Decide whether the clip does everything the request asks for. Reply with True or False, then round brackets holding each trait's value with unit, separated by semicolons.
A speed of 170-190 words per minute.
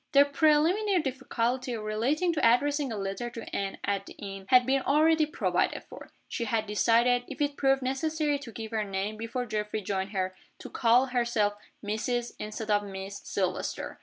True (175 wpm)